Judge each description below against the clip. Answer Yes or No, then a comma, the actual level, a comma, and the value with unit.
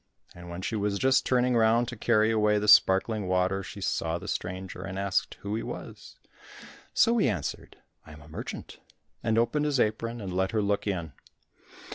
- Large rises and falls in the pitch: No, average, 3.6 semitones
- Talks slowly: No, average, 190 wpm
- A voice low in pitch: Yes, low, 105 Hz